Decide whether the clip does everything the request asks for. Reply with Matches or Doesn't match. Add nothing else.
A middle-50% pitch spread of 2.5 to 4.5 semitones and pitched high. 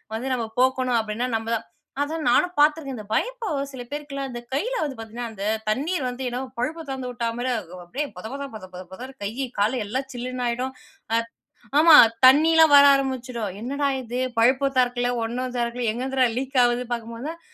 Matches